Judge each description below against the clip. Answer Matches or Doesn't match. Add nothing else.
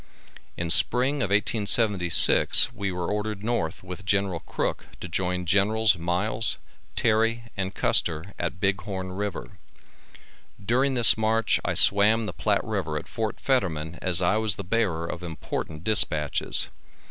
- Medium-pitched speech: Doesn't match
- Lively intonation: Doesn't match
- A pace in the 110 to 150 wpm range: Matches